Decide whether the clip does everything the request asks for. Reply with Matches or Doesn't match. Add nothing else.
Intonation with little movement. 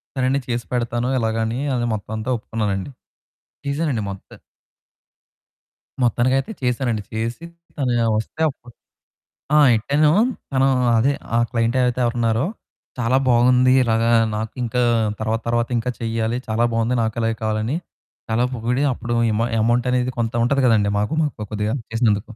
Matches